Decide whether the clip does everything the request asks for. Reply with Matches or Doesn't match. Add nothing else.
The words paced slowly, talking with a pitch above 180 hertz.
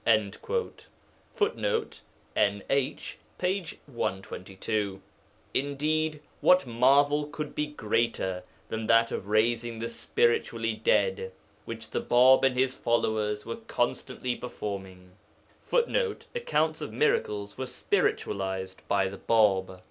Doesn't match